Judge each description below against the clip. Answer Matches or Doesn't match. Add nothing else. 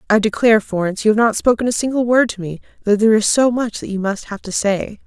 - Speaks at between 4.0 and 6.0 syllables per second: Doesn't match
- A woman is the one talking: Matches